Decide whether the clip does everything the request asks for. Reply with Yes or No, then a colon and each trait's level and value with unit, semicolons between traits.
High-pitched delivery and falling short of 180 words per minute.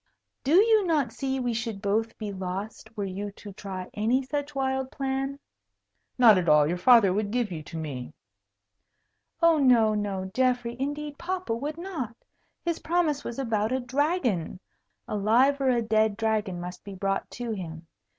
Yes: high, 230 Hz; average, 170 wpm